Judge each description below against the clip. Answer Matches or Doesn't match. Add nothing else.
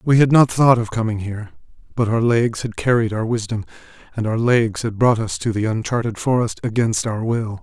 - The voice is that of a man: Matches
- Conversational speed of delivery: Doesn't match